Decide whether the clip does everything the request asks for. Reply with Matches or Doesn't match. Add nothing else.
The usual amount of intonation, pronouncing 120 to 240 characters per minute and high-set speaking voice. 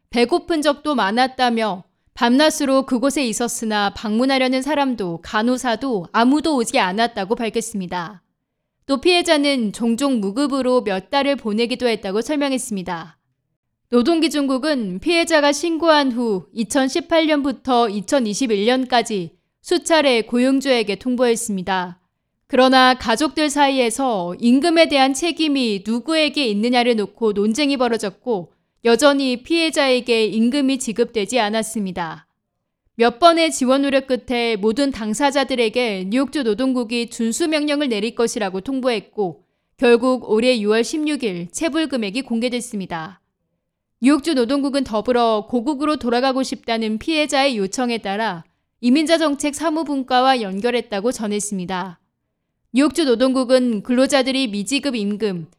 Doesn't match